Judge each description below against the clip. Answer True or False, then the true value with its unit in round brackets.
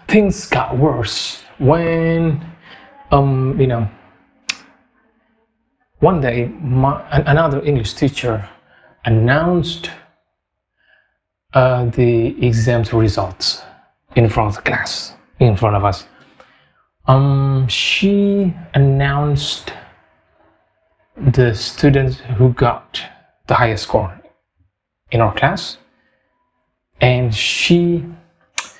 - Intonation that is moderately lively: False (6.2 semitones)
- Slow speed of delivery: True (90 wpm)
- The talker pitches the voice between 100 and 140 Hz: True (135 Hz)